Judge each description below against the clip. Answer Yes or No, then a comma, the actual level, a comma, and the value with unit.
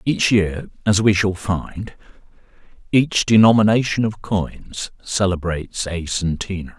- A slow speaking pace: Yes, slow, 115 wpm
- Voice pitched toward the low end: Yes, low, 100 Hz